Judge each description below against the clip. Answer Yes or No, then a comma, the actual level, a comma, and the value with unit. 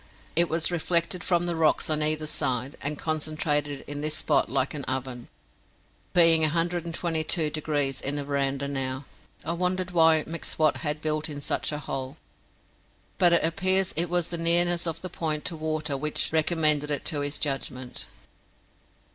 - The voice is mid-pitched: Yes, medium, 155 Hz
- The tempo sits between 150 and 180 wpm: Yes, average, 165 wpm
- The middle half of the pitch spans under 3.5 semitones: Yes, narrow, 2.6 semitones